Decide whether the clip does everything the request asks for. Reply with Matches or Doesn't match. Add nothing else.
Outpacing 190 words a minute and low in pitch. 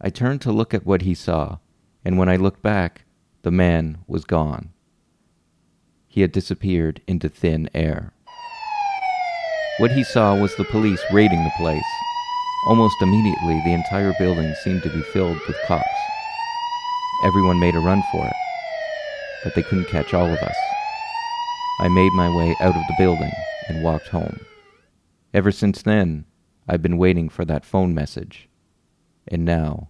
Doesn't match